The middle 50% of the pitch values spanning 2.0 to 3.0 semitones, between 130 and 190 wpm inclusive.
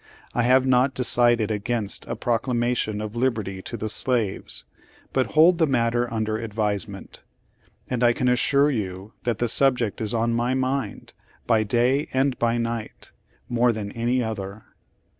Yes: narrow, 2.6 semitones; average, 160 wpm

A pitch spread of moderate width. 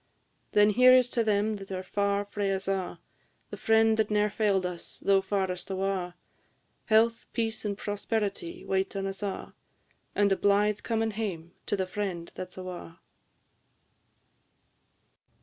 No: narrow, 2.0 semitones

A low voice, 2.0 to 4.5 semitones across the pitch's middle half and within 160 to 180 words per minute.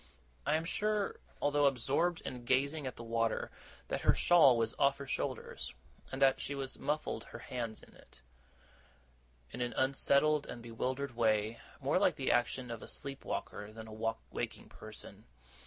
Yes: low, 130 Hz; average, 3.4 semitones; average, 170 wpm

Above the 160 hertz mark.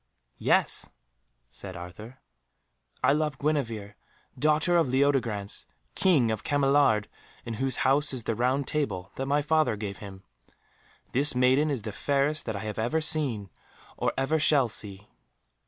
No: low, 130 Hz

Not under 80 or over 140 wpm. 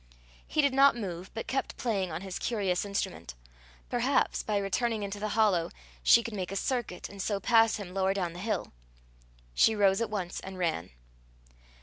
No: average, 185 wpm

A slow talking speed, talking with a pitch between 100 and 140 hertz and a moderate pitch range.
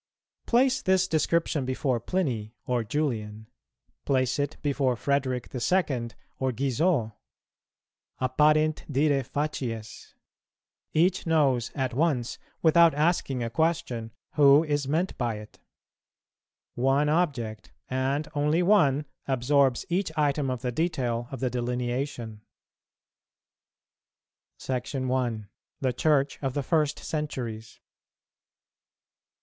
Yes: slow, 110 wpm; low, 135 Hz; average, 3.8 semitones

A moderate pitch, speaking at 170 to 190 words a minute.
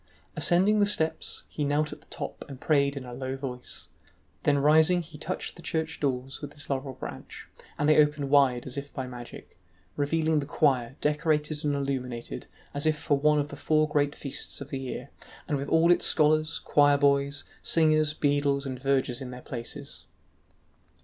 Yes: medium, 145 Hz; average, 185 wpm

